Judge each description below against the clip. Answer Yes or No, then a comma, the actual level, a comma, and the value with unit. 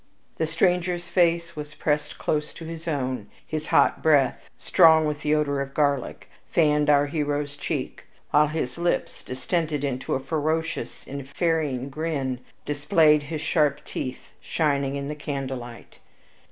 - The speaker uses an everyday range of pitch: No, narrow, 2.3 semitones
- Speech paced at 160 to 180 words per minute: No, average, 145 wpm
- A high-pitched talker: No, medium, 150 Hz